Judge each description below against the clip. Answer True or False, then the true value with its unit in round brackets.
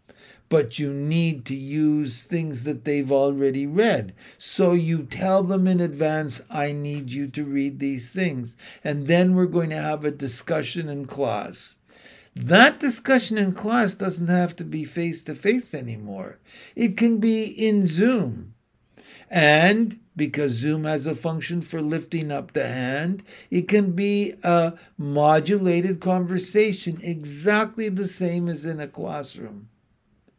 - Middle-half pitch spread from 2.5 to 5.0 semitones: True (4.7 semitones)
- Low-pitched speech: False (165 Hz)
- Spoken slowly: False (145 wpm)